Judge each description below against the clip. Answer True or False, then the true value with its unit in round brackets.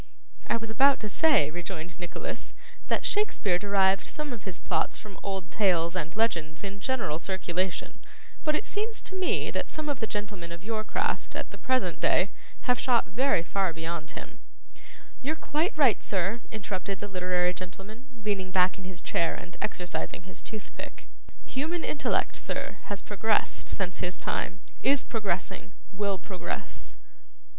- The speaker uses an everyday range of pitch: True (4.4 semitones)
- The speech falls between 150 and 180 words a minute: True (165 wpm)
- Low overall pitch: False (195 Hz)